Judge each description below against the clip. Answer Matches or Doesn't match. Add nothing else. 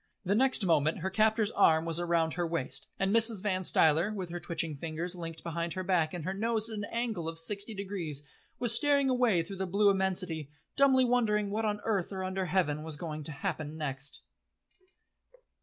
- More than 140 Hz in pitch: Matches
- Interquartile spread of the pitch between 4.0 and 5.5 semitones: Matches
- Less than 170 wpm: Doesn't match